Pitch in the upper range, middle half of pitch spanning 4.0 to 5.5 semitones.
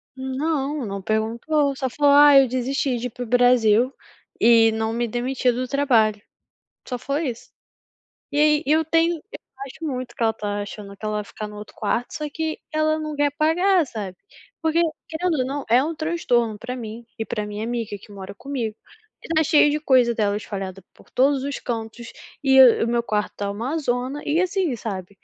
Yes: very high, 250 Hz; average, 4.9 semitones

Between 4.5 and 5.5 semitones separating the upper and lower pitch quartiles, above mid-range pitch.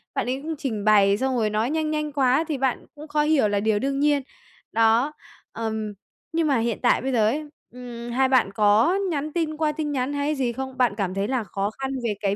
Yes: average, 5.1 semitones; very high, 260 Hz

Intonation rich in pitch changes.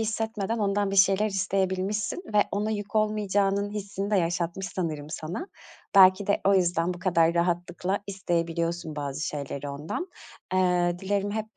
No: average, 3.0 semitones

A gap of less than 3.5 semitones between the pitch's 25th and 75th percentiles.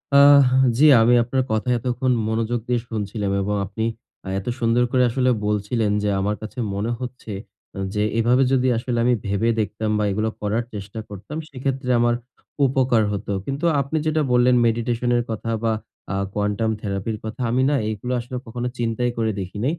Yes: average, 3.0 semitones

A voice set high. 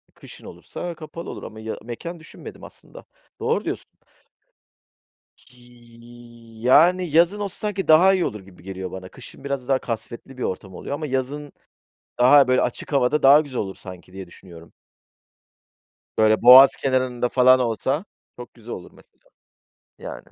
No: low, 125 Hz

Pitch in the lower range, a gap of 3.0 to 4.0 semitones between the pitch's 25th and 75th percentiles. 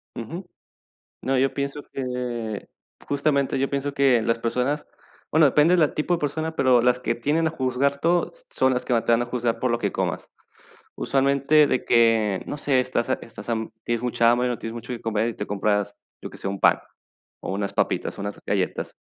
Yes: low, 125 Hz; average, 3.4 semitones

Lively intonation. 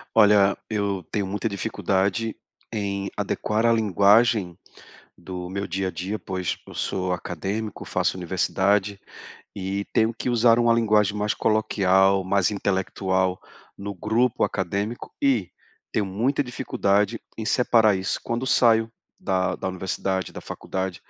No: average, 2.7 semitones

